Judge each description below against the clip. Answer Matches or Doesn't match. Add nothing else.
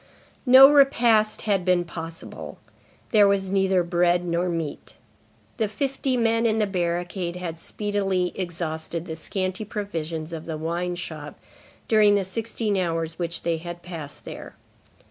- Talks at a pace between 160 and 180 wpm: Doesn't match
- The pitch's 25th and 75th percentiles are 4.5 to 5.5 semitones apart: Doesn't match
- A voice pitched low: Doesn't match